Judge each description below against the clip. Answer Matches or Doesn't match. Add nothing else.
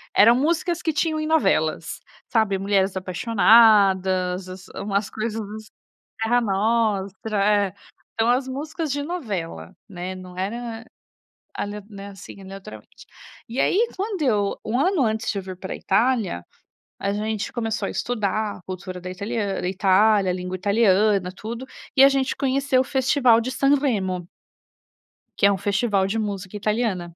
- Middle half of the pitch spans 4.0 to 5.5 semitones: Matches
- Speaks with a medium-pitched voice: Doesn't match